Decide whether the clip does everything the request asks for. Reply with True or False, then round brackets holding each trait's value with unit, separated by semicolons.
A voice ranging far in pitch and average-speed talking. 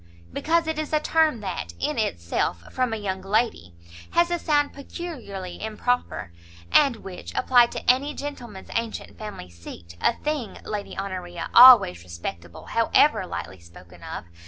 True (8.8 semitones; 150 wpm)